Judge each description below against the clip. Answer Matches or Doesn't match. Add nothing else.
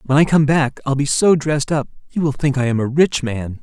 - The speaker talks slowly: Doesn't match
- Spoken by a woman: Doesn't match